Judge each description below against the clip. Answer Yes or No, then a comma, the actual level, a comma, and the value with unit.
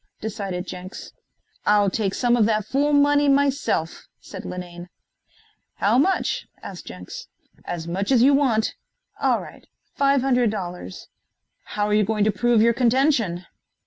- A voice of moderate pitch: No, high, 215 Hz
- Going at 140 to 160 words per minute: Yes, average, 145 wpm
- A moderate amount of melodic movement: No, wide, 6.0 semitones